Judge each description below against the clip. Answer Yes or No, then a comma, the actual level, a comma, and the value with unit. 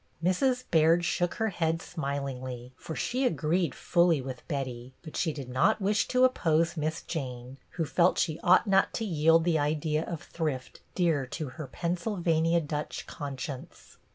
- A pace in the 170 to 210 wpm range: No, average, 160 wpm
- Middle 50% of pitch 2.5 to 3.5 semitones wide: No, average, 3.9 semitones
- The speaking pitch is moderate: Yes, medium, 160 Hz